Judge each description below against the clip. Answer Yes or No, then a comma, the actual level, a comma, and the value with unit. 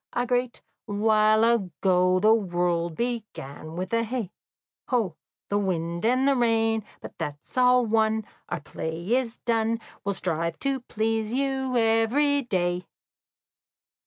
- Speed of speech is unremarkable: No, slow, 130 wpm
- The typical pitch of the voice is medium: No, high, 220 Hz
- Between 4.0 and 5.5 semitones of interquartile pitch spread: Yes, average, 4.9 semitones